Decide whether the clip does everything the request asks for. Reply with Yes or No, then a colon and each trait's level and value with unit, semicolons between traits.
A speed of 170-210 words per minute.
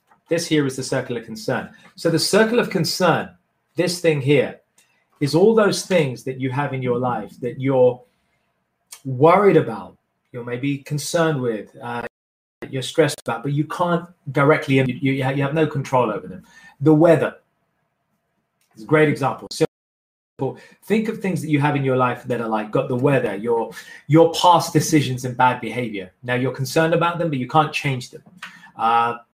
Yes: average, 180 wpm